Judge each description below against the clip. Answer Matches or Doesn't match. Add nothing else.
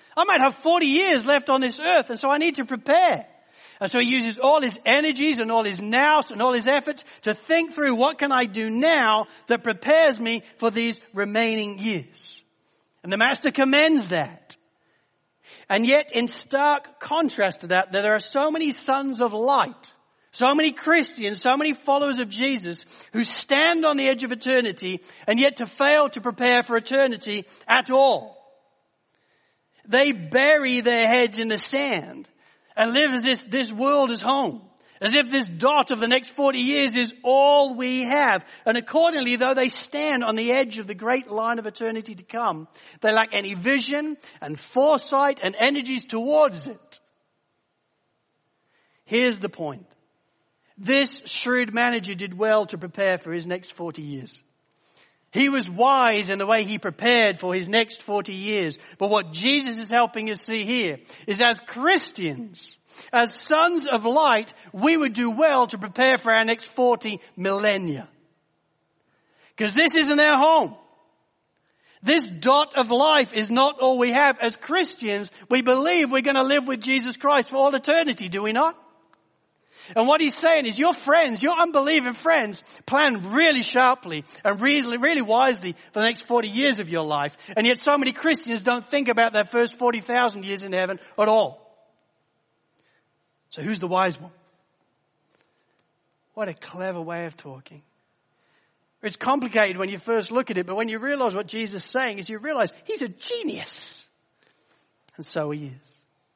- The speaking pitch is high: Matches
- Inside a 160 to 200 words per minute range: Matches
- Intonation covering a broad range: Doesn't match